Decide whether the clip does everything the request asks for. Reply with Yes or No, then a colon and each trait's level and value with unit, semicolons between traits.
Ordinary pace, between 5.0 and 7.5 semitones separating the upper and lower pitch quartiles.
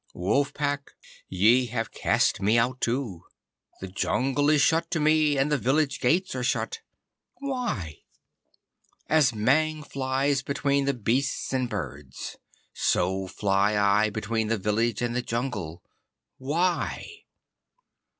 No: slow, 130 wpm; wide, 5.4 semitones